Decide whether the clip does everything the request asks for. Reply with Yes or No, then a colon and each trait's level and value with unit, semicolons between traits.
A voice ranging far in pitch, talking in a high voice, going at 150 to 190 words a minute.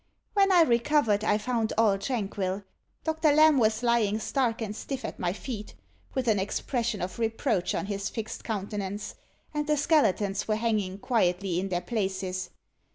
No: average, 4.0 semitones; high, 215 Hz; average, 160 wpm